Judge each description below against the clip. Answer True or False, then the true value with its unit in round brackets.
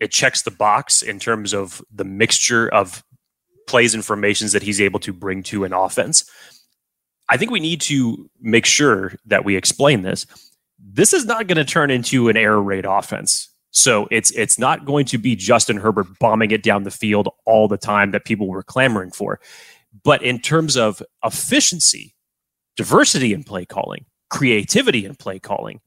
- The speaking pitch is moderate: False (110 Hz)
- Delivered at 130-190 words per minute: True (180 wpm)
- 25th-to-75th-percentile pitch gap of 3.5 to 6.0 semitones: True (4.2 semitones)